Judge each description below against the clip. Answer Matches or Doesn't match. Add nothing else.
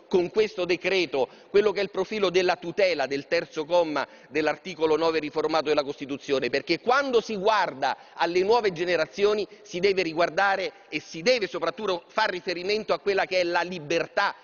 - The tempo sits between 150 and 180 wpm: Matches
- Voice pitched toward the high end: Doesn't match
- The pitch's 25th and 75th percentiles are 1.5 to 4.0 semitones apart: Matches